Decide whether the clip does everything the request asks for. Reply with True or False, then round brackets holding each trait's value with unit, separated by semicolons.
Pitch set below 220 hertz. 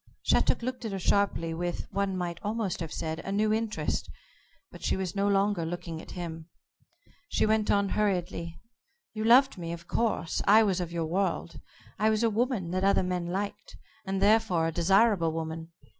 True (190 Hz)